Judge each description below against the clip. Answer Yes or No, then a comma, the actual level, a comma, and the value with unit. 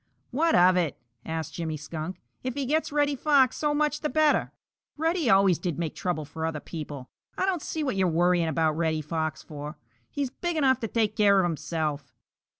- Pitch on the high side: No, medium, 180 Hz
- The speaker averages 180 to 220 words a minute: Yes, average, 195 wpm